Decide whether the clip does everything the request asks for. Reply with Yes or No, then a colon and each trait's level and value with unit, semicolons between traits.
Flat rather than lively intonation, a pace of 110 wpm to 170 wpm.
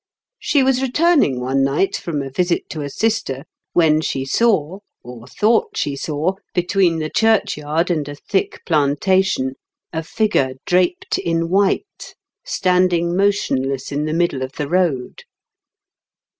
No: average, 5.3 semitones; average, 140 wpm